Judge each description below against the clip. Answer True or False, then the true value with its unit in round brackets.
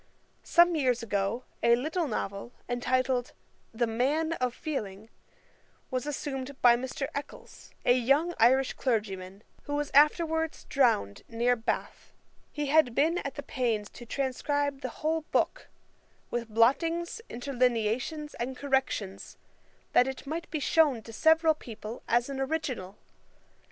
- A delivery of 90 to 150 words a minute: True (135 wpm)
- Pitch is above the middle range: True (260 Hz)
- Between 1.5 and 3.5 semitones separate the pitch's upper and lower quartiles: False (4.1 semitones)